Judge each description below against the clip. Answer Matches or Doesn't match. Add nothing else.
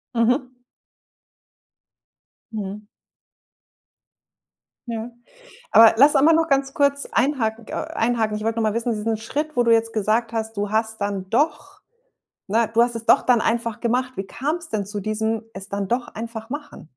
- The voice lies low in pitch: Doesn't match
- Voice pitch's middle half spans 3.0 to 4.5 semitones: Doesn't match